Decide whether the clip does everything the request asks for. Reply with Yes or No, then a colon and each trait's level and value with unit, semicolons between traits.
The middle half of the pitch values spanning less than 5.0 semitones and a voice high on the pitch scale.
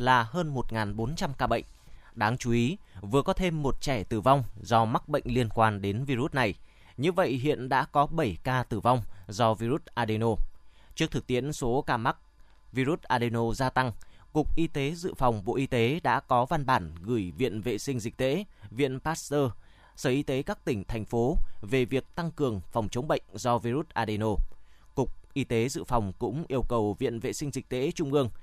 No: average, 3.9 semitones; low, 125 Hz